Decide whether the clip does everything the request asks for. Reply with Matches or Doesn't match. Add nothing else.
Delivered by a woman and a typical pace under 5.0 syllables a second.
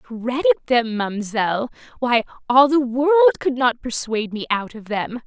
Matches